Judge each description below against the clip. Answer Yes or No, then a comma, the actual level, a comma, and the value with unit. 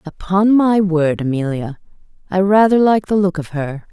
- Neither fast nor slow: Yes, average, 170 wpm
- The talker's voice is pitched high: No, medium, 180 Hz